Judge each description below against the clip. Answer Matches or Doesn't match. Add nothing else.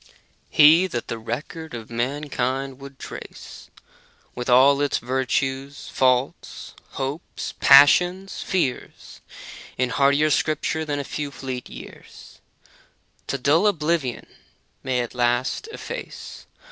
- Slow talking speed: Matches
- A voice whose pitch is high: Doesn't match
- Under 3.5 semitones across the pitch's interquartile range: Matches